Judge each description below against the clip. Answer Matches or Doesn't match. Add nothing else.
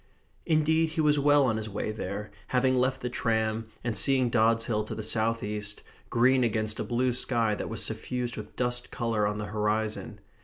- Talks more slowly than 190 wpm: Doesn't match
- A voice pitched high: Doesn't match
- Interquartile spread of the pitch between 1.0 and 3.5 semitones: Matches